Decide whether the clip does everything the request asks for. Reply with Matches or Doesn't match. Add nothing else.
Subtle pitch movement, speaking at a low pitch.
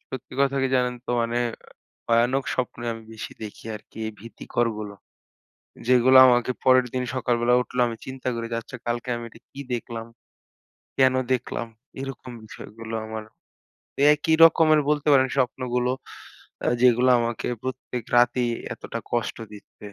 Matches